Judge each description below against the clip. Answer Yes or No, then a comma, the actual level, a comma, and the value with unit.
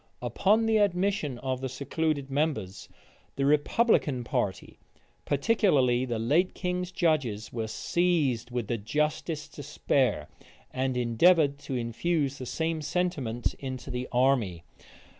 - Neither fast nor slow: No, slow, 120 wpm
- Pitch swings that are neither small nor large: Yes, average, 5.0 semitones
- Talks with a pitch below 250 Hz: Yes, medium, 140 Hz